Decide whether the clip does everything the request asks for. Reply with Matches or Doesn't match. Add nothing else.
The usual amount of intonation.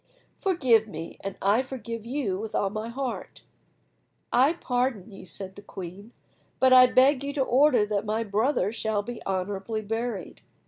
Matches